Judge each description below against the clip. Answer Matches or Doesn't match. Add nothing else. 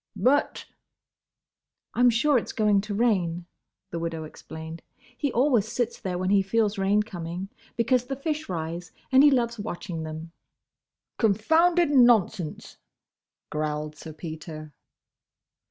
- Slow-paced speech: Matches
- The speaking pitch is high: Matches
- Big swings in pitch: Matches